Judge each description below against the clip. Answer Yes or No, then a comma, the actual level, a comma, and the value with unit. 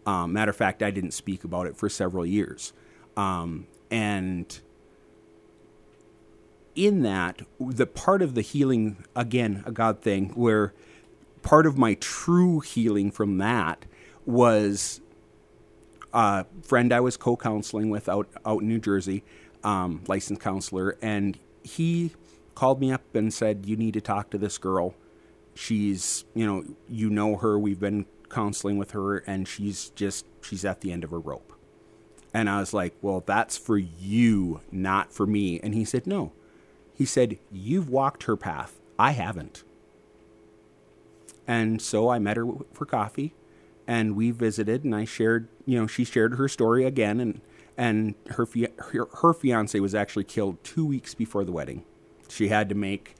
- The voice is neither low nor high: No, low, 110 Hz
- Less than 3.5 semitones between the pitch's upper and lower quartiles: Yes, average, 2.9 semitones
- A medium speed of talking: Yes, average, 165 wpm